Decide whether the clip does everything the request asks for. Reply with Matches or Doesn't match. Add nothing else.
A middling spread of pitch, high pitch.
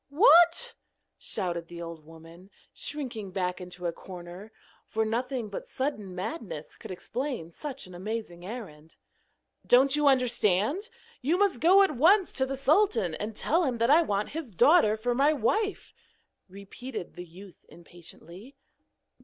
Doesn't match